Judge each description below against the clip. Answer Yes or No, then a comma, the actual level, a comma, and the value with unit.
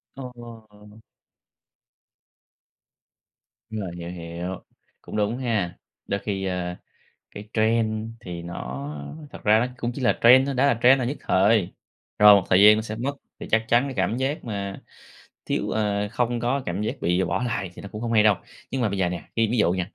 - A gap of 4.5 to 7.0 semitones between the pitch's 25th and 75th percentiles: No, average, 4.0 semitones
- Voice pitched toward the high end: No, low, 105 Hz